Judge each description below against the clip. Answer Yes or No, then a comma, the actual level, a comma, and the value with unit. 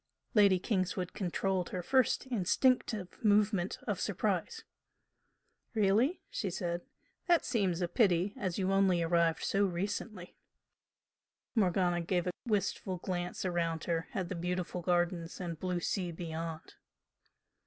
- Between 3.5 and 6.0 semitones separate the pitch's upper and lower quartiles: No, narrow, 2.6 semitones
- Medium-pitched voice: Yes, medium, 180 Hz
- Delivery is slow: Yes, slow, 130 wpm